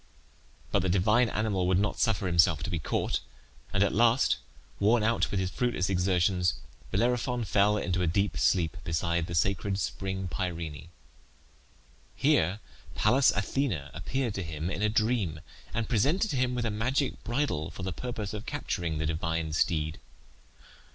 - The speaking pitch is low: Yes, very low, 95 Hz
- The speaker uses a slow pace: No, average, 160 wpm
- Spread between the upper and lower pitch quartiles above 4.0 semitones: Yes, average, 4.9 semitones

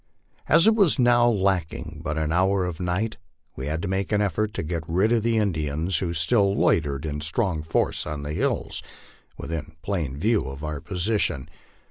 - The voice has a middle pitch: No, very low, 90 Hz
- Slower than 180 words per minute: No, average, 185 wpm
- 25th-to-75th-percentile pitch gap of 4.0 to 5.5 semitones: Yes, average, 5.2 semitones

